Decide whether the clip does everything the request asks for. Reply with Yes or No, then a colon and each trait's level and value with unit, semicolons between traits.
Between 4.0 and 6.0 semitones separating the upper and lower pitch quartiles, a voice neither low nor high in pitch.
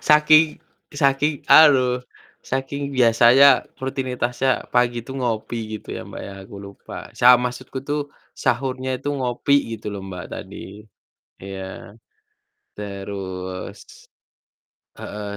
No: average, 4.4 semitones; low, 125 Hz